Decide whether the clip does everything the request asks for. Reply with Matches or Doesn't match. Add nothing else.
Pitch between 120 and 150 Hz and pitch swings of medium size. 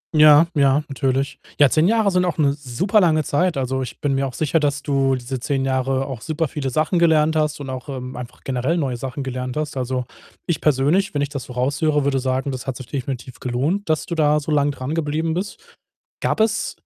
Matches